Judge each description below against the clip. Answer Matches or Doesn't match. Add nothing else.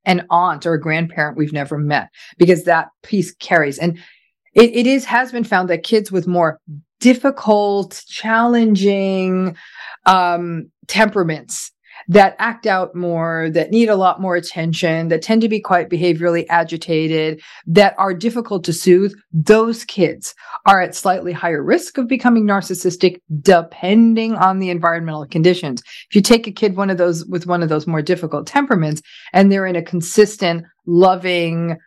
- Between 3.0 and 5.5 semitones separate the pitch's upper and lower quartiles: Matches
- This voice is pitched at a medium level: Matches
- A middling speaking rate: Matches